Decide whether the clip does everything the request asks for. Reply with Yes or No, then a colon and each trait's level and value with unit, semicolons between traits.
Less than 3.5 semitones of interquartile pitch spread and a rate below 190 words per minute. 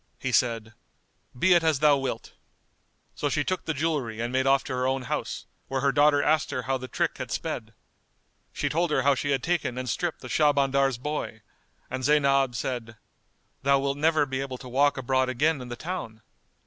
No: narrow, 2.5 semitones; average, 200 wpm